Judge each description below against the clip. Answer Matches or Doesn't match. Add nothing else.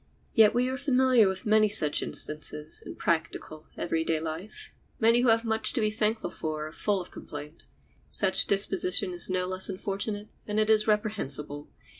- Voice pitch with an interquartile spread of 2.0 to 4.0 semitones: Doesn't match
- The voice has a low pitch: Doesn't match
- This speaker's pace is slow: Doesn't match